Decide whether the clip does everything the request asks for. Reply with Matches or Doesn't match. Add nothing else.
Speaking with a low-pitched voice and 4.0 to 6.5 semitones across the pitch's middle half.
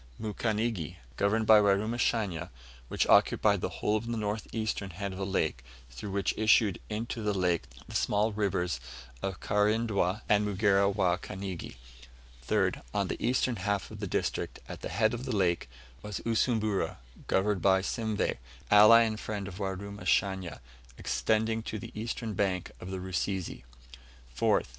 Doesn't match